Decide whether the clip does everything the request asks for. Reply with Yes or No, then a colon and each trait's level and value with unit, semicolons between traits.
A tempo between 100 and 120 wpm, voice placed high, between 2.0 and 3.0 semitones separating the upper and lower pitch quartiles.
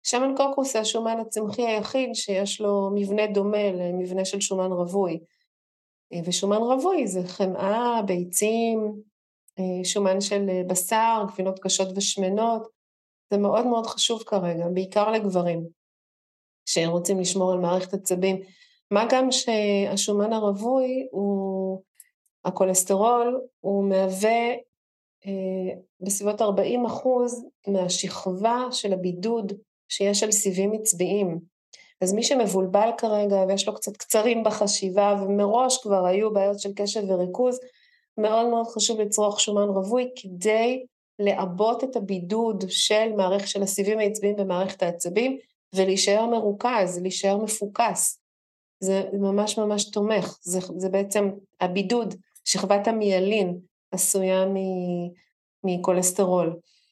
Yes: average, 110 wpm; high, 200 Hz; average, 2.7 semitones